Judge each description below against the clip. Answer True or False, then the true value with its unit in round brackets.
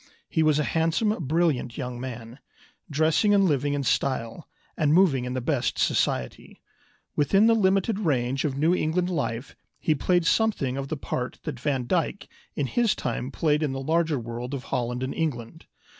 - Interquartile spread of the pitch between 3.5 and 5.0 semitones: True (4.7 semitones)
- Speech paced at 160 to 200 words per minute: True (175 wpm)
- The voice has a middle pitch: True (145 Hz)